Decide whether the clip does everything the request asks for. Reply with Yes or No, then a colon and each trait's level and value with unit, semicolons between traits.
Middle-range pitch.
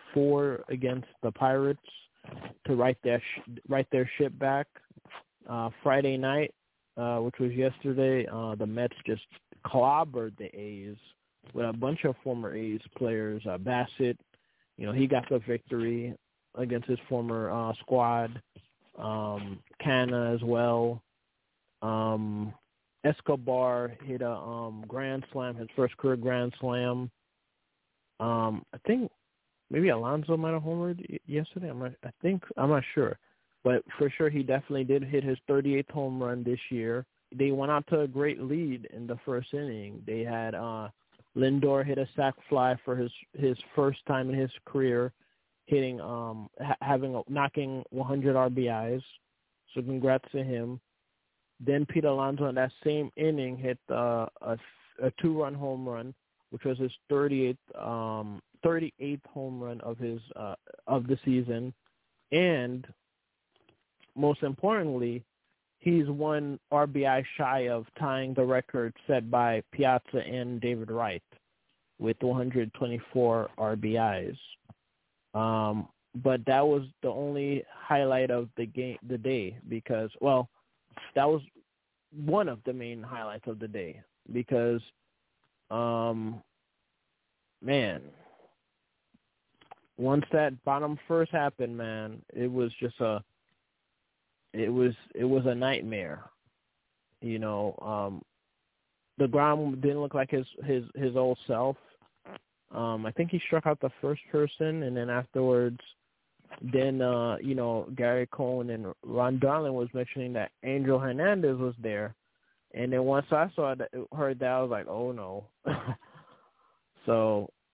No: low, 125 Hz